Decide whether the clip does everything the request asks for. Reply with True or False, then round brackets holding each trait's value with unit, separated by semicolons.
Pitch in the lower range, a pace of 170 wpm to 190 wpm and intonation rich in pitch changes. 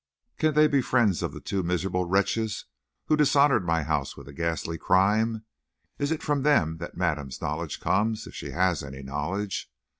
True (95 Hz; 180 wpm; 5.8 semitones)